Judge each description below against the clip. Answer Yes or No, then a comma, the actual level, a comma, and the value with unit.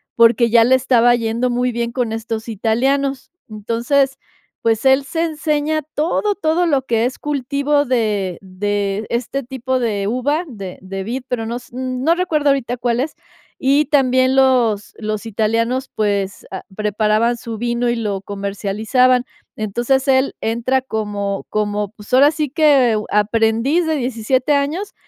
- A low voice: No, high, 240 Hz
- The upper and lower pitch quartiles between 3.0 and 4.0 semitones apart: Yes, average, 3.7 semitones